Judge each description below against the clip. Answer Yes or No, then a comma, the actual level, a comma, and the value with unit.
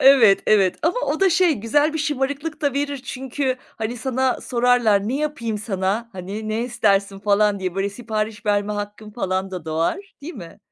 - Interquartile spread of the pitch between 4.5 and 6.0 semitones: Yes, average, 5.2 semitones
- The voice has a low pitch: No, high, 225 Hz